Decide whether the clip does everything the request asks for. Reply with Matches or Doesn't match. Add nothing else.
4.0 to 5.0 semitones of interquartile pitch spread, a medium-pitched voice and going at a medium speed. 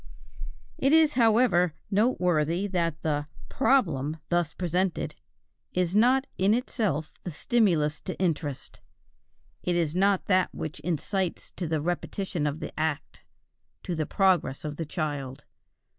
Doesn't match